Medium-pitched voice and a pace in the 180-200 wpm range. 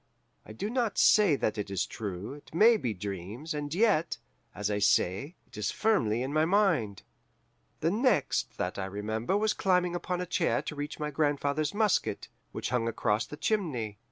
Yes: medium, 145 Hz; average, 185 wpm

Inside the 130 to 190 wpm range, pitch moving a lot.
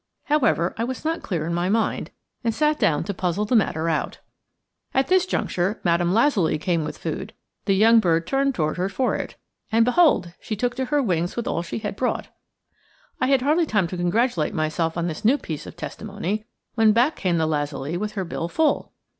No: fast, 205 wpm; wide, 6.5 semitones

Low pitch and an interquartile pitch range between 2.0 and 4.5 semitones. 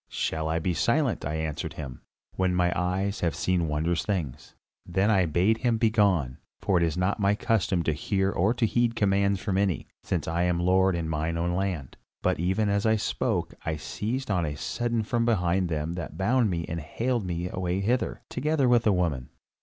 Yes: very low, 95 Hz; average, 4.2 semitones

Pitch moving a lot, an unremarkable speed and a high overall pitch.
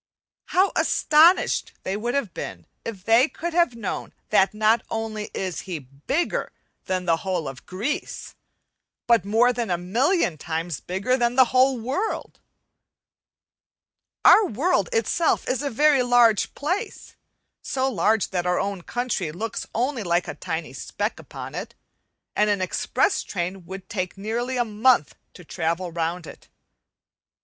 Yes: wide, 6.1 semitones; average, 150 wpm; high, 220 Hz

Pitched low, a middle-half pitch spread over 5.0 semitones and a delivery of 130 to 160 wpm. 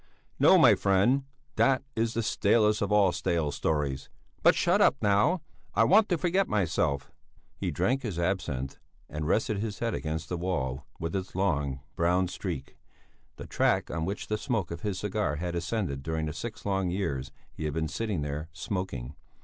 No: very low, 90 Hz; wide, 5.4 semitones; average, 180 wpm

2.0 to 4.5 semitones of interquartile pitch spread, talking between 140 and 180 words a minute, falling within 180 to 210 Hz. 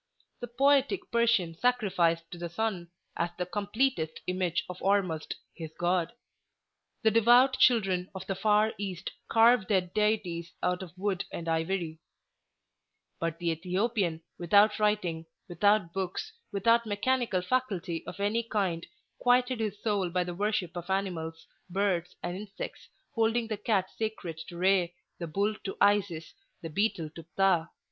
Yes: average, 4.0 semitones; average, 145 wpm; high, 190 Hz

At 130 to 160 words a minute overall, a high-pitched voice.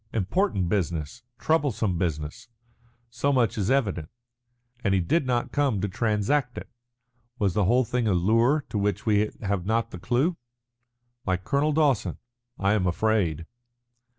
No: average, 150 wpm; low, 110 Hz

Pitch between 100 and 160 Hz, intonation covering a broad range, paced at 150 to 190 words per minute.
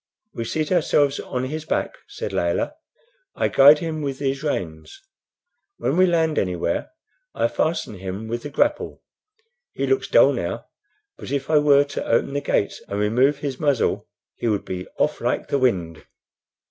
Yes: medium, 140 Hz; wide, 5.9 semitones; average, 165 wpm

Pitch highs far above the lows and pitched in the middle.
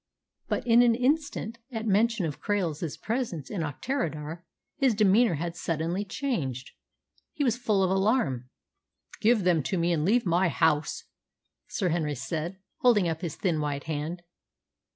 Yes: wide, 6.3 semitones; medium, 180 Hz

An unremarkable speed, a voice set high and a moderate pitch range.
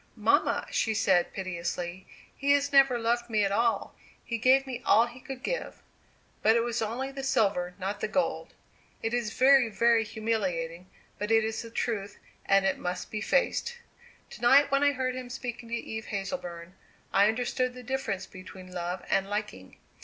Yes: average, 180 wpm; high, 225 Hz; average, 4.5 semitones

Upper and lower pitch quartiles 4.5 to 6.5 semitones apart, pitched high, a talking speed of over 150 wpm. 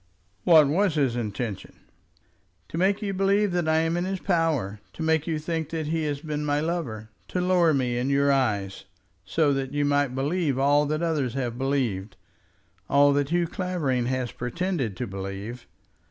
No: average, 4.8 semitones; medium, 145 Hz; average, 180 wpm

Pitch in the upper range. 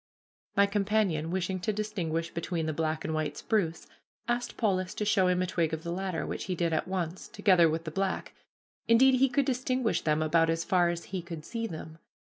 No: medium, 180 Hz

